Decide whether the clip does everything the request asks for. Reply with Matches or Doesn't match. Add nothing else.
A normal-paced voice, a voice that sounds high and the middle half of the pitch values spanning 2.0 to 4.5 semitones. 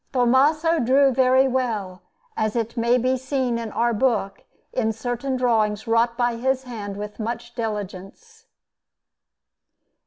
Doesn't match